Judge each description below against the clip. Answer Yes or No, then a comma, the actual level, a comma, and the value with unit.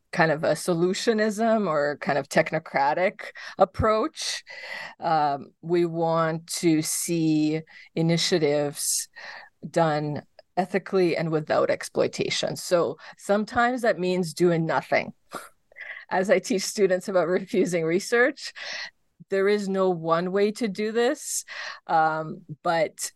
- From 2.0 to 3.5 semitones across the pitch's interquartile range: No, average, 4.2 semitones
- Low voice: No, medium, 180 Hz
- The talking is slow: Yes, slow, 110 wpm